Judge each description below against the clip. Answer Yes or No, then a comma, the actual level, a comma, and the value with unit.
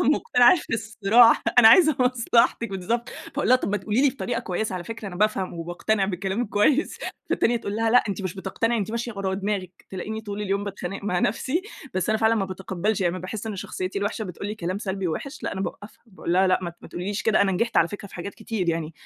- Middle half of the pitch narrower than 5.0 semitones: Yes, average, 3.3 semitones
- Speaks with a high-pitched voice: Yes, high, 205 Hz